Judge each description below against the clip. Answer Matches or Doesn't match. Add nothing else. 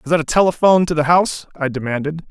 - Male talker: Matches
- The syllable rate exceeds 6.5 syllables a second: Matches